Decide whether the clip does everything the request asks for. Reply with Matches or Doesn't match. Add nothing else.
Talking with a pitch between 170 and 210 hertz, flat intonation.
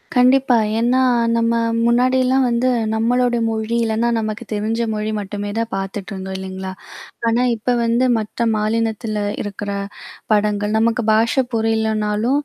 Doesn't match